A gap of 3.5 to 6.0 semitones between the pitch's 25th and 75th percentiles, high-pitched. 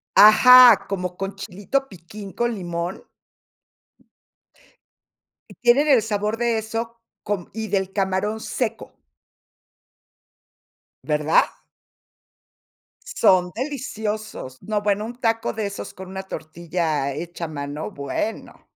Yes: average, 4.1 semitones; high, 205 Hz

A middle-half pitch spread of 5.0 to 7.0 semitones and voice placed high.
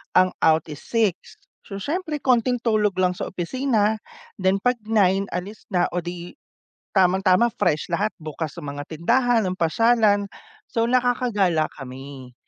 Yes: average, 5.3 semitones; high, 195 Hz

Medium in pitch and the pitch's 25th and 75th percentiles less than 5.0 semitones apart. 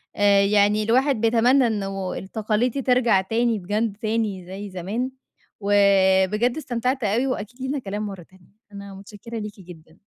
No: high, 210 Hz; average, 3.3 semitones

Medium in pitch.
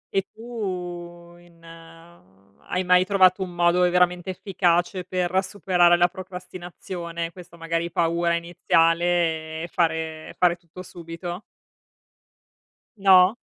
Yes: medium, 175 Hz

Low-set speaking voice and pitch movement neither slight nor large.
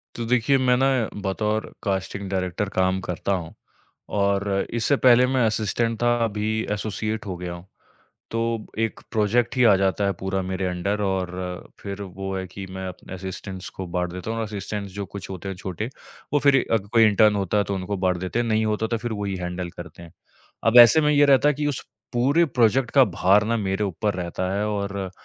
Yes: low, 100 Hz; average, 3.2 semitones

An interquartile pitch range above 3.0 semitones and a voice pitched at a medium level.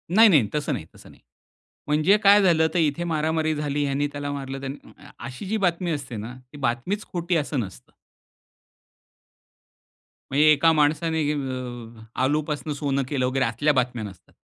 Yes: average, 3.5 semitones; medium, 145 Hz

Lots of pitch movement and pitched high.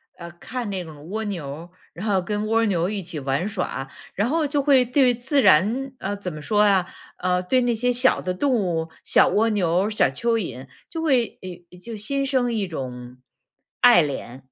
Yes: wide, 6.1 semitones; high, 205 Hz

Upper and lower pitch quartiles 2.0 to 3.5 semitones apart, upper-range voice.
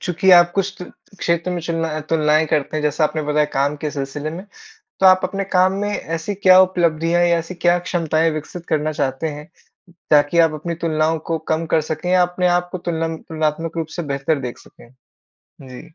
No: narrow, 2.4 semitones; medium, 165 Hz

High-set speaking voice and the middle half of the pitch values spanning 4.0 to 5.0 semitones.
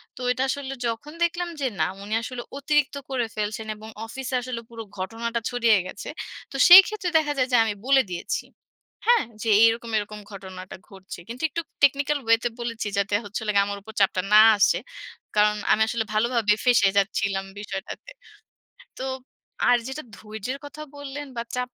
Yes: high, 230 Hz; average, 4.3 semitones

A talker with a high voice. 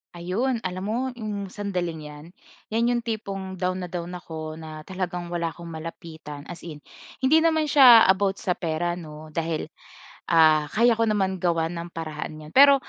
No: medium, 180 Hz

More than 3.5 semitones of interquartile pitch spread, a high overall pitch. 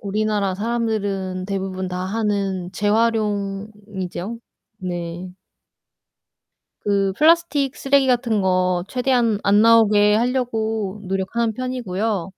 No: average, 3.2 semitones; high, 210 Hz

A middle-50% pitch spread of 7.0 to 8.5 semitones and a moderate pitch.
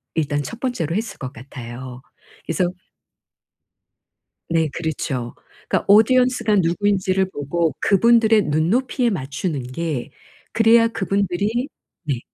Yes: wide, 7.4 semitones; medium, 175 Hz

